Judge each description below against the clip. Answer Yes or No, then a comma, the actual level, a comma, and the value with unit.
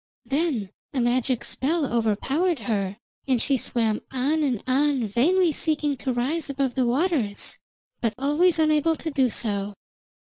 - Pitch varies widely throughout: No, average, 4.6 semitones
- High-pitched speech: Yes, very high, 265 Hz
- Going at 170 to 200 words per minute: No, average, 145 wpm